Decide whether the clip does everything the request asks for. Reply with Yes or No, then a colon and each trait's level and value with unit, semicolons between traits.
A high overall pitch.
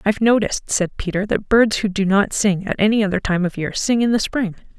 Yes: high, 205 Hz